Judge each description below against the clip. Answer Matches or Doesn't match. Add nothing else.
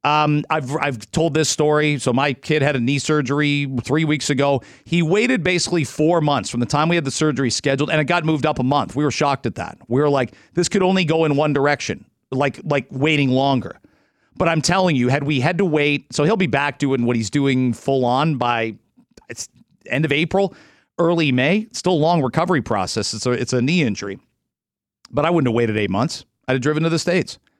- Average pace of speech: Doesn't match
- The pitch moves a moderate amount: Matches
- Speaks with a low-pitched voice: Doesn't match